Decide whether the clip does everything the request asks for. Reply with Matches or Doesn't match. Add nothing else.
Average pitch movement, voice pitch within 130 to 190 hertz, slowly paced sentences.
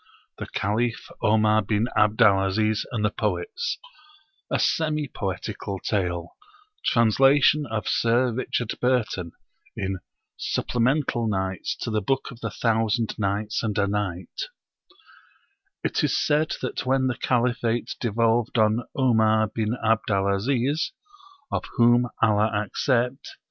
Doesn't match